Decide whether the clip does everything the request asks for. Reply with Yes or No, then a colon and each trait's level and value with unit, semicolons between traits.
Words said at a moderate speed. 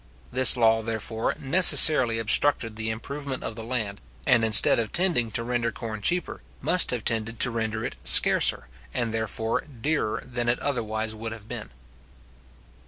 Yes: average, 160 wpm